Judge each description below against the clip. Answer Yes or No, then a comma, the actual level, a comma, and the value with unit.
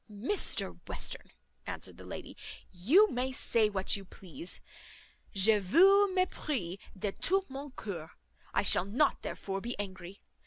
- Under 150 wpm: Yes, average, 140 wpm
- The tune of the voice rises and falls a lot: Yes, wide, 7.7 semitones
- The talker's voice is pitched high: Yes, high, 210 Hz